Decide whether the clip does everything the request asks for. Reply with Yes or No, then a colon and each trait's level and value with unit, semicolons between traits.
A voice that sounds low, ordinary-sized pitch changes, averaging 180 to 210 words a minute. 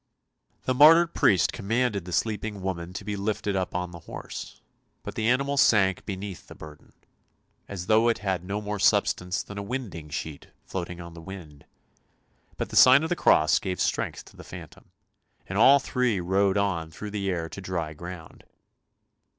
Yes: very low, 95 Hz; average, 3.7 semitones; average, 185 wpm